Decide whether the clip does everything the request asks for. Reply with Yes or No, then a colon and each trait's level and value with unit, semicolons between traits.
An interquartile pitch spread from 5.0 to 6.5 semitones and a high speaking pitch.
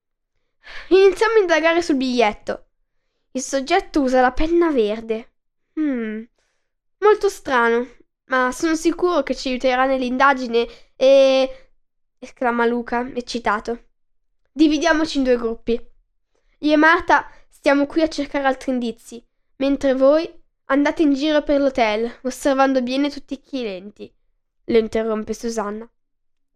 No: average, 4.2 semitones; very high, 265 Hz